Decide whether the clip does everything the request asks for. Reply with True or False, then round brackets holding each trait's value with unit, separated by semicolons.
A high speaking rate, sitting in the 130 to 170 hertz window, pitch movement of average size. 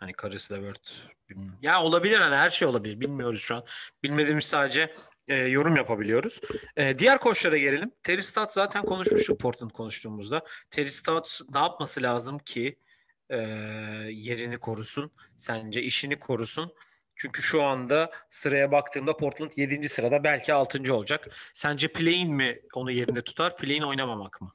True (145 wpm; 140 Hz; 4.8 semitones)